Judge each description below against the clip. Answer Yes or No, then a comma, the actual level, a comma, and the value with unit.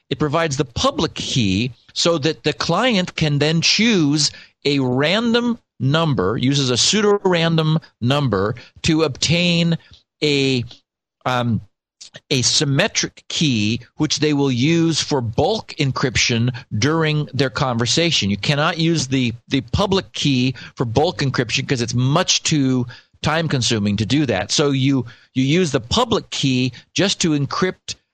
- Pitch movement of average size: Yes, average, 4.2 semitones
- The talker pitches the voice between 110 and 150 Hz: Yes, medium, 140 Hz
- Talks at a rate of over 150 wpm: No, average, 140 wpm